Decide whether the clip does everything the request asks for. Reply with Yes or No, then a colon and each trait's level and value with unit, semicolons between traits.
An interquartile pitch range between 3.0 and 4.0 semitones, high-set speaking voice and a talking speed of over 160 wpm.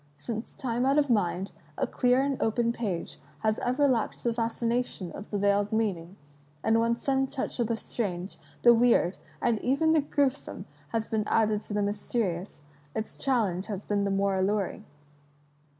Yes: average, 3.5 semitones; high, 225 Hz; average, 170 wpm